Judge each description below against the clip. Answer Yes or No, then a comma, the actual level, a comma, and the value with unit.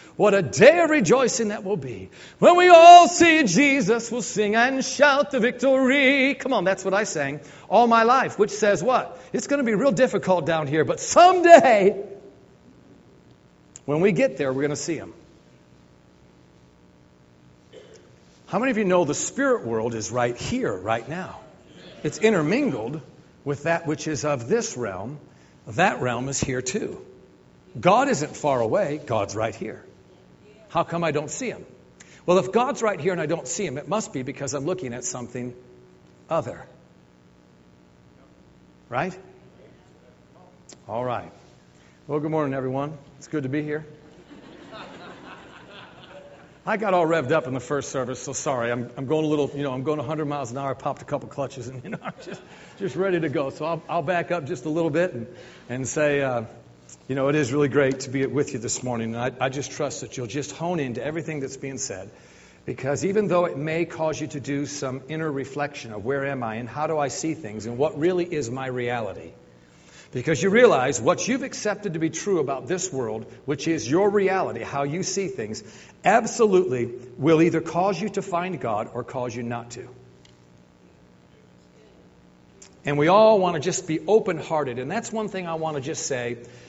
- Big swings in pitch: Yes, wide, 7.6 semitones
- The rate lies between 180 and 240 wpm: Yes, average, 190 wpm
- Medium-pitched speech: Yes, medium, 145 Hz